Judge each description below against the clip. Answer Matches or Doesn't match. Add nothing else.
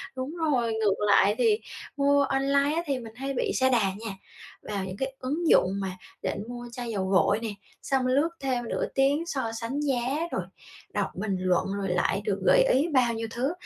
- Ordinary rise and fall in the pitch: Matches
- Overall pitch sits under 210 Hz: Doesn't match